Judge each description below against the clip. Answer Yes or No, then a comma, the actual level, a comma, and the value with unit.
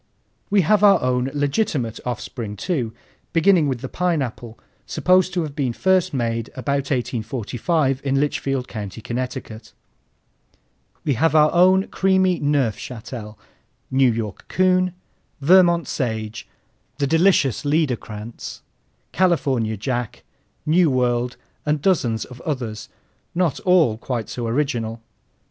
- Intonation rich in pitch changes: Yes, wide, 6.1 semitones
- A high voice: No, low, 135 Hz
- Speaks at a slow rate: Yes, slow, 115 wpm